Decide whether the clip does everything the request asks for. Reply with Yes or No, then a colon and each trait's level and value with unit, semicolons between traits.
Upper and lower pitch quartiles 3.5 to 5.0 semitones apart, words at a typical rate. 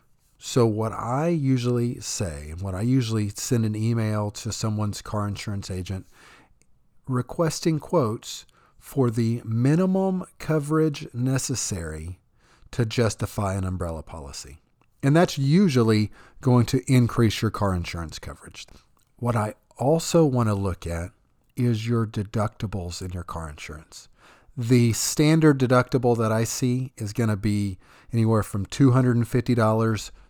No: average, 4.2 semitones; slow, 130 wpm